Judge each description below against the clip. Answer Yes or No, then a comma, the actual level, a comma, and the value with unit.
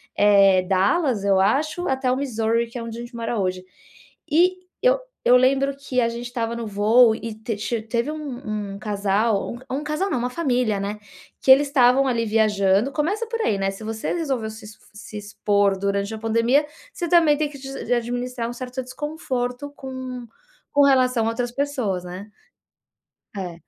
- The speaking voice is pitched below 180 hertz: No, high, 240 Hz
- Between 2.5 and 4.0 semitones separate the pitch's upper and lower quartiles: No, average, 4.4 semitones